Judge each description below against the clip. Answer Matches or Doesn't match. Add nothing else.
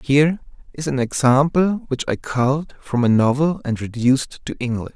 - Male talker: Matches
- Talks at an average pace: Matches